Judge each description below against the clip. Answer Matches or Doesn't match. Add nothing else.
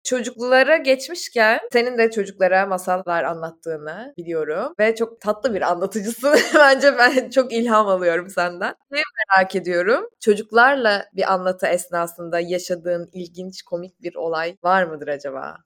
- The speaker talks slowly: Doesn't match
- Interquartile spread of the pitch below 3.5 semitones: Doesn't match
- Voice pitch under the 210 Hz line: Matches